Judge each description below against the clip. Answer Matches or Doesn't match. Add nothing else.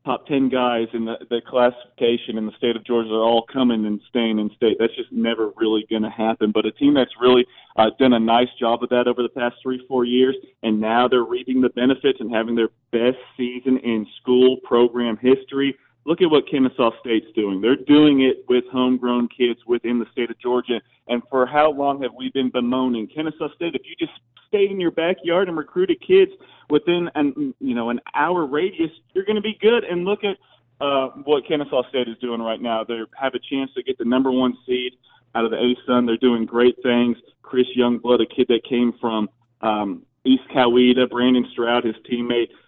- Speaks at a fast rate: Matches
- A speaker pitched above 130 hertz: Doesn't match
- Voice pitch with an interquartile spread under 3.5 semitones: Matches